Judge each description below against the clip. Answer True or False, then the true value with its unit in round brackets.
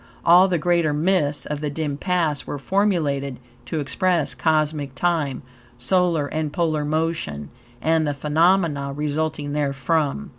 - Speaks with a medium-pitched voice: True (150 Hz)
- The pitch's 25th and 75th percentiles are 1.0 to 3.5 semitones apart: True (2.8 semitones)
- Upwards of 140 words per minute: False (135 wpm)